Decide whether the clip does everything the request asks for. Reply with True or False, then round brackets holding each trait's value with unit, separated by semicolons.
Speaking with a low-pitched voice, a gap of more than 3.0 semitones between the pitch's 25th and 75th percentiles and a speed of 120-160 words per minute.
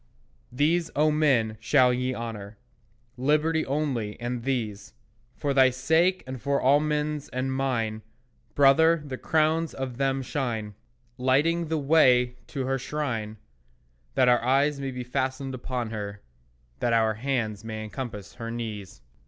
True (130 Hz; 3.9 semitones; 145 wpm)